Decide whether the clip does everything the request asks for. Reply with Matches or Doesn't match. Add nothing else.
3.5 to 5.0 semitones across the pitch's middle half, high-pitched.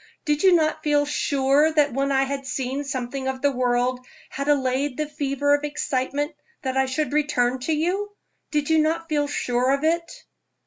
Doesn't match